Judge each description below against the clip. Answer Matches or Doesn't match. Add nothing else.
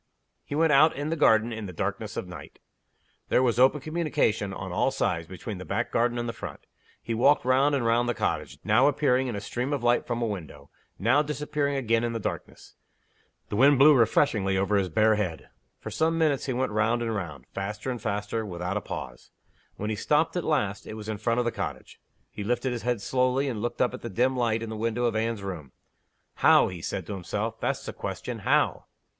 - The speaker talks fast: Matches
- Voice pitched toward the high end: Doesn't match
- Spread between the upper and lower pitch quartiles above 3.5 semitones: Matches